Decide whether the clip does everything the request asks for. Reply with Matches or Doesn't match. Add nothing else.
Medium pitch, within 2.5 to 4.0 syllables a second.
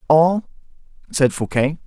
Matches